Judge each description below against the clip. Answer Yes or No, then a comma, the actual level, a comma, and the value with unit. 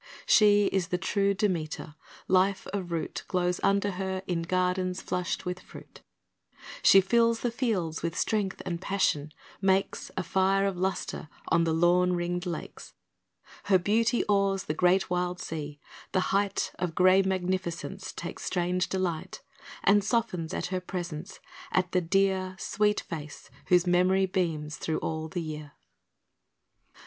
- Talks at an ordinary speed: Yes, average, 145 wpm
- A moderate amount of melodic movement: No, narrow, 2.0 semitones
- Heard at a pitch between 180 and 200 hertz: Yes, medium, 185 Hz